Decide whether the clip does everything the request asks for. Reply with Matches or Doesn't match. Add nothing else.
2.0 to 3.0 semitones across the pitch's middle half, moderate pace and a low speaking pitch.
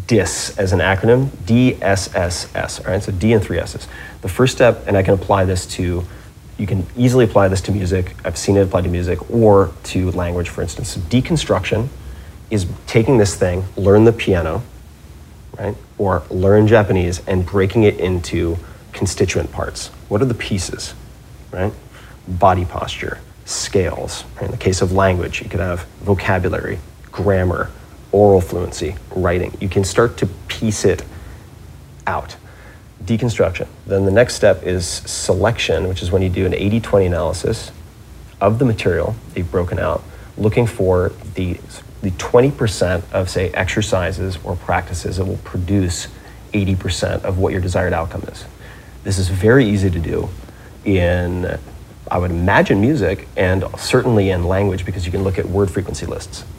Matches